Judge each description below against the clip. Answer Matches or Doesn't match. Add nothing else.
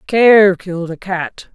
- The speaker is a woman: Matches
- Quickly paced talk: Doesn't match